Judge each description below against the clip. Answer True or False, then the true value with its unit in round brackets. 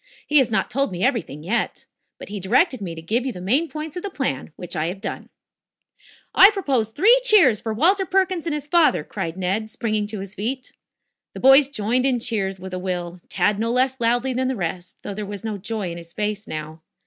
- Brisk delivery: True (230 wpm)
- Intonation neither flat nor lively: False (6.1 semitones)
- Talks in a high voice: True (220 Hz)